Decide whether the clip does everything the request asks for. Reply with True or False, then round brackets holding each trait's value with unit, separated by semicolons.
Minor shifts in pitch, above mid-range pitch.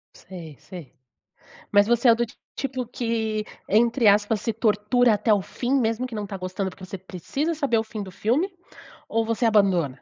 False (3.3 semitones; 220 Hz)